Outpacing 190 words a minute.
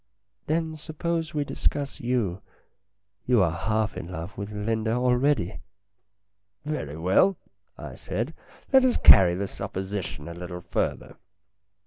No: average, 140 wpm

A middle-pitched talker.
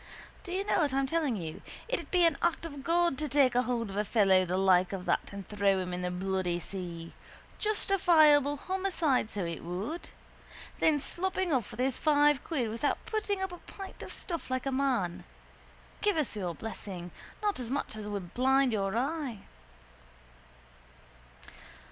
No: very high, 255 Hz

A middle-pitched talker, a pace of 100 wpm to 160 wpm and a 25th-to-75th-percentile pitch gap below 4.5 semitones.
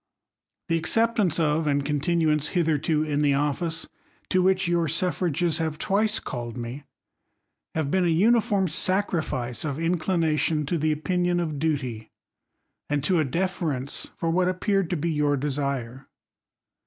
Yes: medium, 160 Hz; average, 145 wpm; average, 3.6 semitones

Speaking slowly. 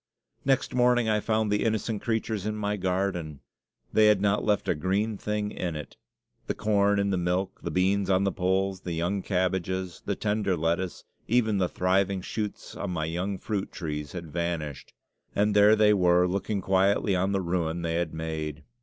No: average, 185 wpm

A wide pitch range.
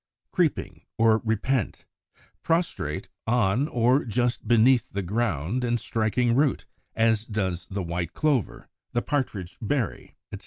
No: average, 3.8 semitones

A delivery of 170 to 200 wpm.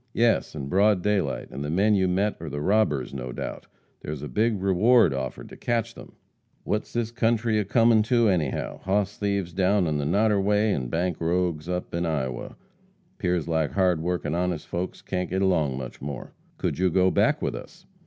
Yes: average, 195 wpm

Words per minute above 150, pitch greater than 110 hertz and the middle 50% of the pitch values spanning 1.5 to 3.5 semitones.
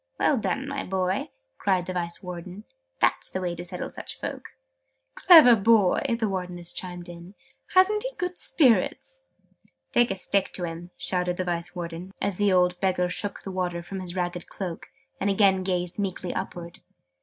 Yes: average, 175 wpm; medium, 185 Hz; narrow, 2.4 semitones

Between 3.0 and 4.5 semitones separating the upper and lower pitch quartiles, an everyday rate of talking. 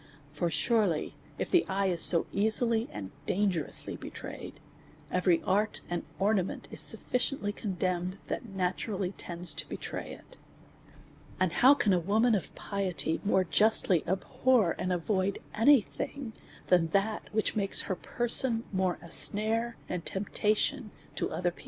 Yes: average, 3.5 semitones; average, 150 wpm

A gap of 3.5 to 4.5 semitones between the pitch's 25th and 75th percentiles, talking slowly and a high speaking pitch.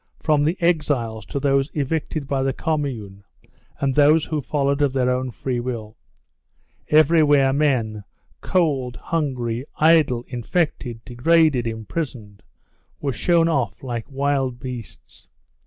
No: average, 3.9 semitones; slow, 125 wpm; low, 135 Hz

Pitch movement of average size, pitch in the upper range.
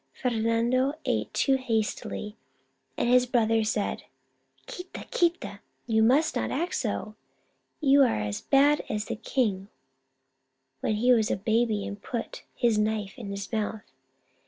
Yes: average, 3.3 semitones; high, 225 Hz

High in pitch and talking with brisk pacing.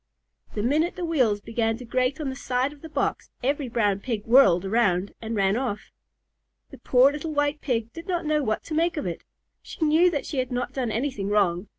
Yes: very high, 250 Hz; fast, 220 wpm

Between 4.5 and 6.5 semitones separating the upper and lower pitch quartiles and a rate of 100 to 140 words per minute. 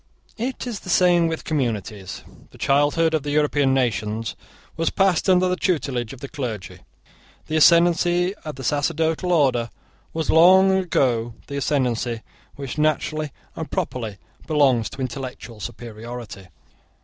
Yes: wide, 5.6 semitones; slow, 135 wpm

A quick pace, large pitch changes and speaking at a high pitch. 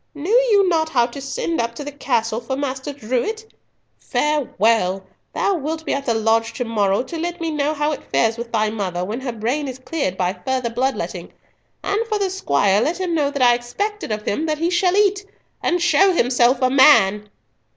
Yes: fast, 215 wpm; wide, 6.4 semitones; very high, 265 Hz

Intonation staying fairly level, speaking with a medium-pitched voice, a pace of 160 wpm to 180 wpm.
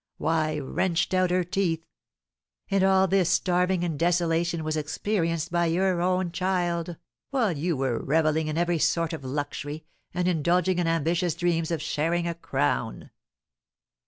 No: narrow, 2.1 semitones; medium, 170 Hz; average, 150 wpm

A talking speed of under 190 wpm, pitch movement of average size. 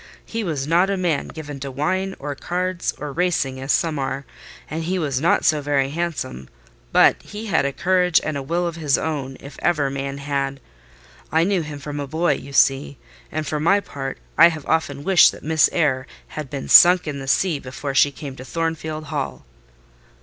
No: average, 200 wpm; average, 3.5 semitones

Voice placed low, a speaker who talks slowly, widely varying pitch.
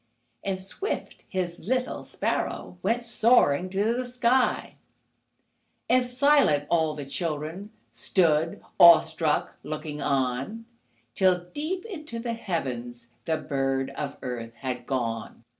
No: medium, 170 Hz; slow, 115 wpm; wide, 9.0 semitones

